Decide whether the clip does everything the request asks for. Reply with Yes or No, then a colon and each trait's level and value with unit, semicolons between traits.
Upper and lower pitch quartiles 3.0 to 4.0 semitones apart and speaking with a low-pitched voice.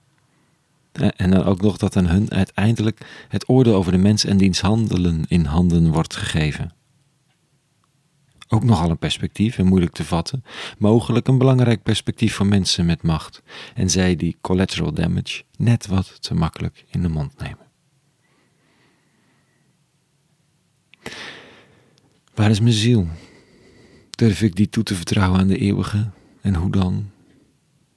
No: average, 4.6 semitones; low, 105 Hz